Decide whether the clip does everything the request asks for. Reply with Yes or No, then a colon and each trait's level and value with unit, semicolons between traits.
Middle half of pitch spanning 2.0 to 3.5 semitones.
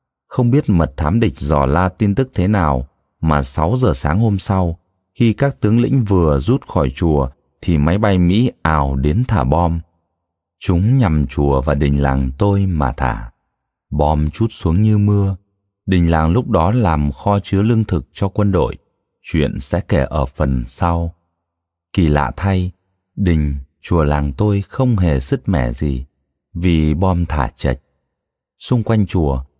No: wide, 5.4 semitones